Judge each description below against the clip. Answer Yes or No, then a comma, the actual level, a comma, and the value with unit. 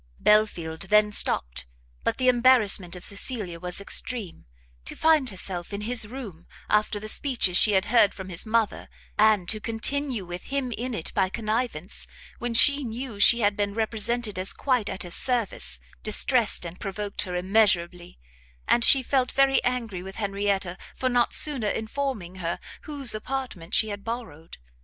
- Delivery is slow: No, average, 165 wpm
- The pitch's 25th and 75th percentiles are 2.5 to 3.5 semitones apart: No, average, 4.5 semitones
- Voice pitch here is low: No, high, 215 Hz